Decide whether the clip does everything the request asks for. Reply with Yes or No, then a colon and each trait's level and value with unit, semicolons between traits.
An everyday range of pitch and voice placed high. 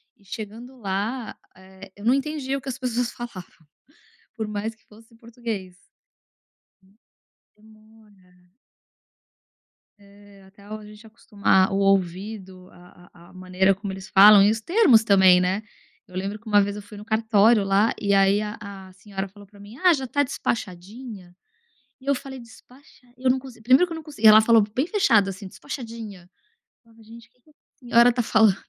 Yes: average, 3.3 semitones; high, 215 Hz